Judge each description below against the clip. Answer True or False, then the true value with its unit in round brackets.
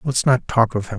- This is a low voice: True (120 Hz)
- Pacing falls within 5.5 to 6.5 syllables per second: False (5.3 syllables/s)